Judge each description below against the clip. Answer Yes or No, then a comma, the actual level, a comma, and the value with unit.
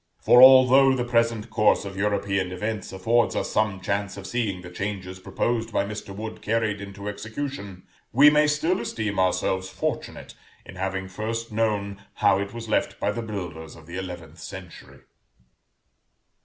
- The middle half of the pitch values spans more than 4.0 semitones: No, average, 3.3 semitones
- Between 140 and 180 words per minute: Yes, average, 160 wpm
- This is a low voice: Yes, low, 100 Hz